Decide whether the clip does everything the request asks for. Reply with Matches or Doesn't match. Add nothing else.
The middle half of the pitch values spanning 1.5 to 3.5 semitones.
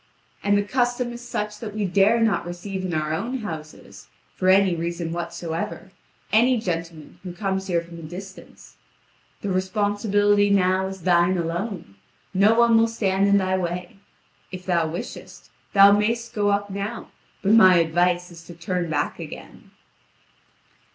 Matches